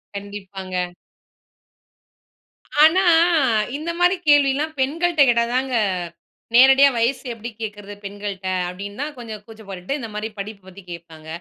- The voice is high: Yes, high, 220 Hz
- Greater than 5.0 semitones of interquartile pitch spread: Yes, wide, 5.6 semitones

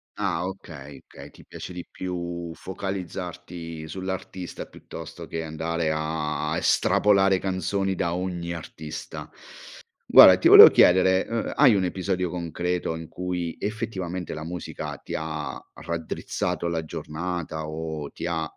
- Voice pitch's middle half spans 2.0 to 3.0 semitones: Yes, narrow, 2.4 semitones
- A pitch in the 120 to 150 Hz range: No, very low, 85 Hz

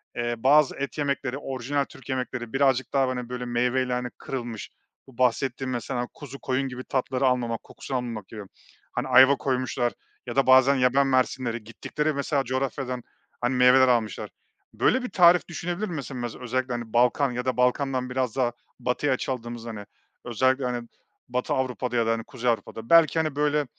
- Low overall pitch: Yes, low, 130 Hz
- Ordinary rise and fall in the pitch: No, narrow, 2.0 semitones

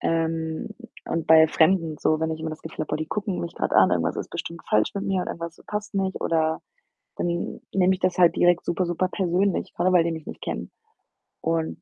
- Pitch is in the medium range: Yes, medium, 170 Hz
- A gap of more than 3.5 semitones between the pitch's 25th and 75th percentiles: No, narrow, 2.4 semitones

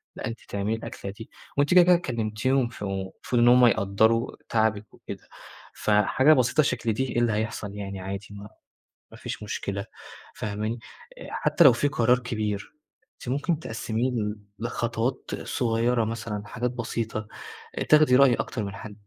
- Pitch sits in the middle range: No, low, 115 Hz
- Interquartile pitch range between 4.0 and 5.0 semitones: No, average, 3.0 semitones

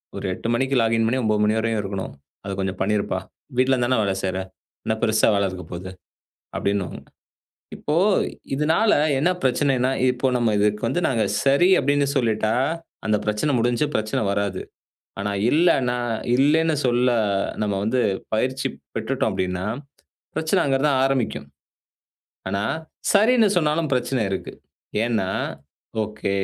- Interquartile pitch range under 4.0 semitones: No, average, 4.7 semitones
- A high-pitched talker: No, low, 120 Hz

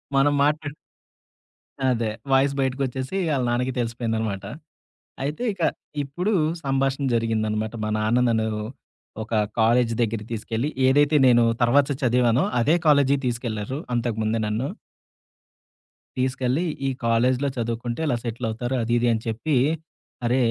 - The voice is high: No, low, 120 Hz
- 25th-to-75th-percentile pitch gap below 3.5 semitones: Yes, average, 3.1 semitones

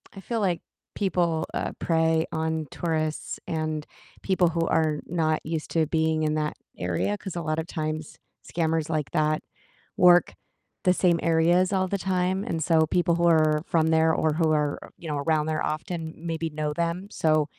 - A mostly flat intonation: Yes, narrow, 1.8 semitones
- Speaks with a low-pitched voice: No, medium, 160 Hz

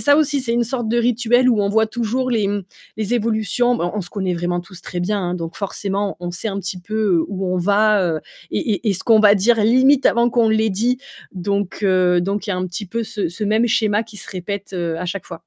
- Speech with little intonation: No, average, 3.8 semitones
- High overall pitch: Yes, high, 205 Hz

